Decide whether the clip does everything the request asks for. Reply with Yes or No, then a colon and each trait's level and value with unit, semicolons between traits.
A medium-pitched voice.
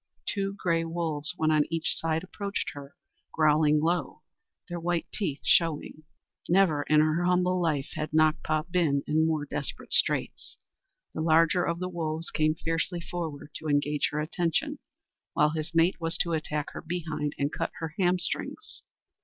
Yes: medium, 160 Hz